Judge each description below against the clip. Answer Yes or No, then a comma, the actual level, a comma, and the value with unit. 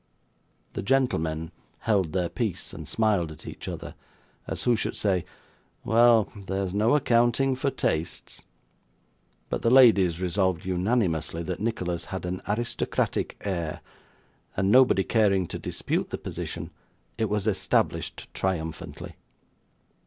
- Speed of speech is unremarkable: No, slow, 125 wpm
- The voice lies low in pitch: Yes, very low, 95 Hz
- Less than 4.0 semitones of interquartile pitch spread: No, average, 4.4 semitones